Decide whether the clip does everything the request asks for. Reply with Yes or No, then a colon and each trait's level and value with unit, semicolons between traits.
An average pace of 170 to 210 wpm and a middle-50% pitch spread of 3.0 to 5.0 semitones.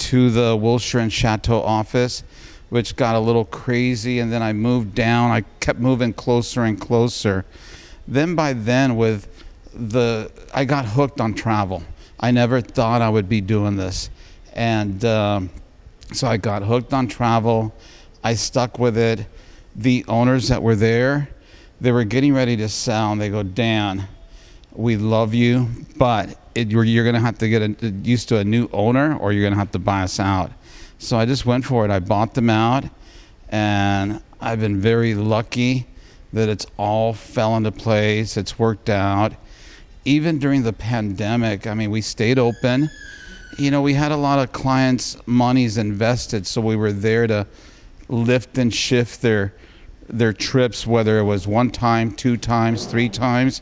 No: average, 175 wpm; narrow, 2.6 semitones